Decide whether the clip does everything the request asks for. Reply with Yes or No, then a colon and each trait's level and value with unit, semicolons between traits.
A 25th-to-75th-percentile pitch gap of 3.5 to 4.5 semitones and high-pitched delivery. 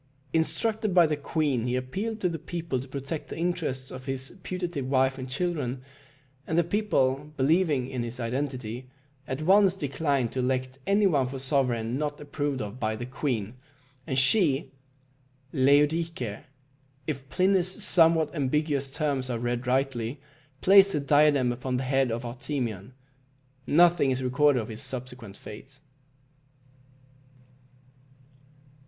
No: average, 4.0 semitones; low, 135 Hz